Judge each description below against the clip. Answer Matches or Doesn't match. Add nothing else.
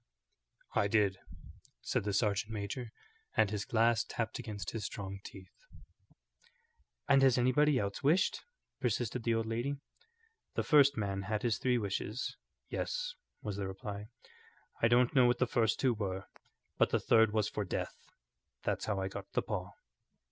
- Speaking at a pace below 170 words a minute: Matches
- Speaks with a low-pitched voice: Matches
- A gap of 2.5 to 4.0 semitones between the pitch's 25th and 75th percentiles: Matches